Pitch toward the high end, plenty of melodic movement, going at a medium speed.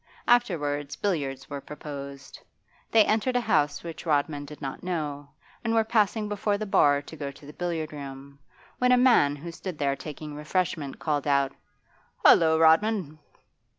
No: medium, 155 Hz; wide, 5.7 semitones; average, 160 wpm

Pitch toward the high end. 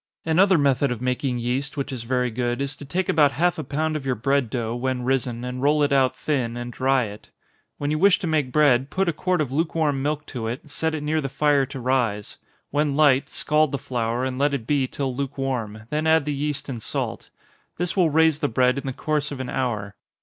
No: medium, 140 Hz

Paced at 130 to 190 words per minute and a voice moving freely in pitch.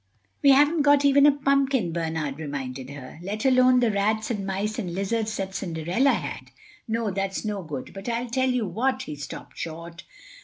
Yes: average, 185 wpm; wide, 7.2 semitones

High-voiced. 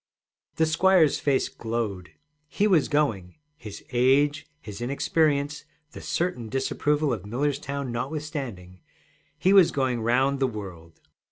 No: low, 135 Hz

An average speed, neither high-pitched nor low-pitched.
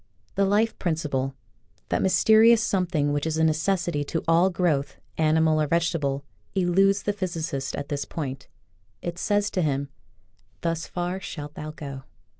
Yes: average, 165 wpm; medium, 165 Hz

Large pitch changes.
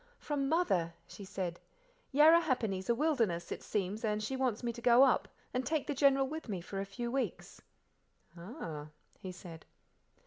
Yes: wide, 6.4 semitones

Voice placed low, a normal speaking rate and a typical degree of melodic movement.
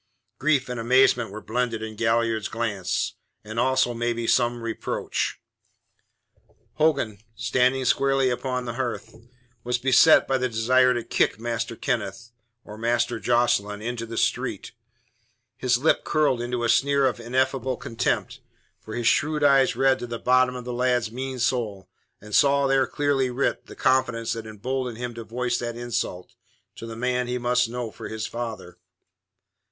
No: low, 120 Hz; average, 160 wpm; narrow, 2.0 semitones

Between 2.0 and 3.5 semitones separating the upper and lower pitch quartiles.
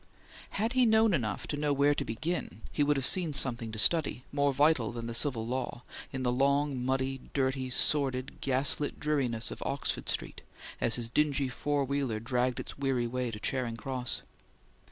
Yes: average, 2.9 semitones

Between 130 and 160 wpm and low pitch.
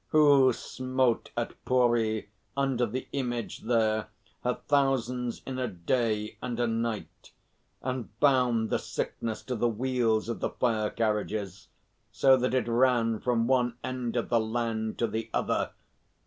Yes: average, 150 wpm; low, 120 Hz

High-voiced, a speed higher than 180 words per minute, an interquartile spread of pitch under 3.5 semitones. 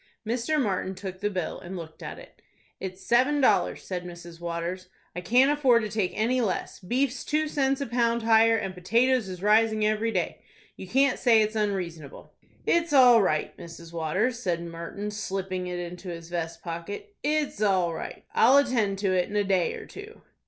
No: high, 205 Hz; average, 190 wpm; average, 5.3 semitones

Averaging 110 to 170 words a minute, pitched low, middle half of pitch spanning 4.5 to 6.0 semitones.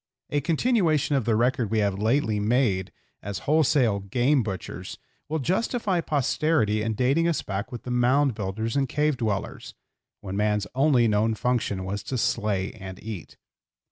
Yes: average, 160 wpm; low, 115 Hz; wide, 5.6 semitones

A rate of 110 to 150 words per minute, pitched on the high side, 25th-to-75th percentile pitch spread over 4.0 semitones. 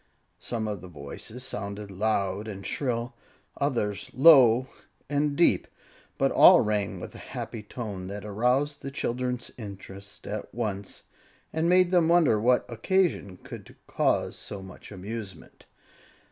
No: slow, 135 wpm; low, 110 Hz; average, 4.5 semitones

